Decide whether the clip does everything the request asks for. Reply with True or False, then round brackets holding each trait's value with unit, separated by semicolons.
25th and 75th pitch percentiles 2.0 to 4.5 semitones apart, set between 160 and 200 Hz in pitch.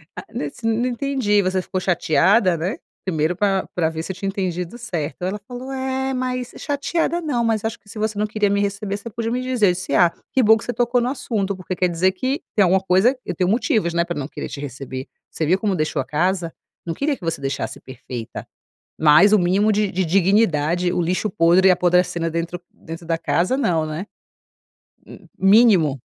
False (4.9 semitones; 190 Hz)